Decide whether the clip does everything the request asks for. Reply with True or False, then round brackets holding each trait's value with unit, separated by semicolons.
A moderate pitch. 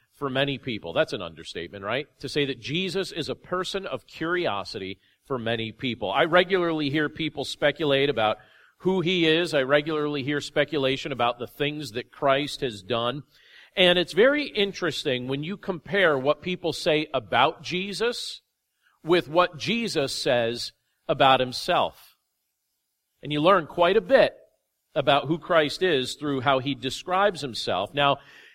True (145 Hz)